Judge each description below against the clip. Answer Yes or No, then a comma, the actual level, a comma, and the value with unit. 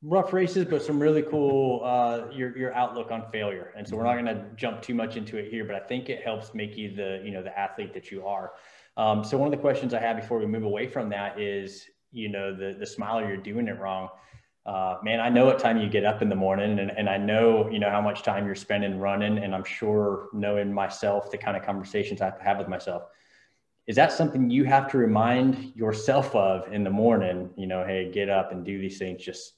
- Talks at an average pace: No, fast, 250 wpm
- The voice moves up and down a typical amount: Yes, average, 3.5 semitones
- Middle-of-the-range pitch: No, low, 105 Hz